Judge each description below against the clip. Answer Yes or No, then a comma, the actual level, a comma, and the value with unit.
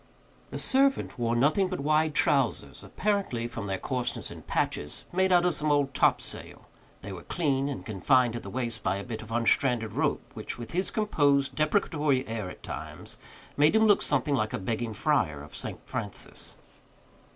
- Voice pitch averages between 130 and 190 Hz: Yes, low, 135 Hz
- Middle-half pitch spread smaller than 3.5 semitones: No, average, 5.2 semitones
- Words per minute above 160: Yes, average, 180 wpm